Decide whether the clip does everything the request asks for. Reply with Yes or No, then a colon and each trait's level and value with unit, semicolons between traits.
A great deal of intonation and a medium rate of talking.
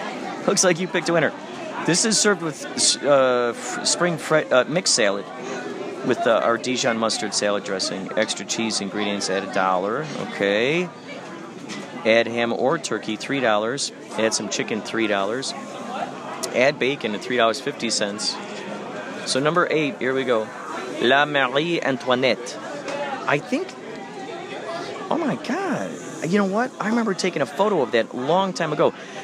Yes: wide, 8.8 semitones; average, 150 wpm